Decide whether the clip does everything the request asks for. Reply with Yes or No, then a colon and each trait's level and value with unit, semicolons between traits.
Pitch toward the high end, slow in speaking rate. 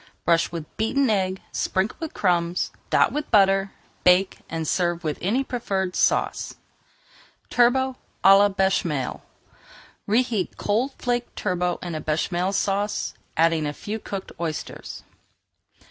Yes: high, 195 Hz; slow, 130 wpm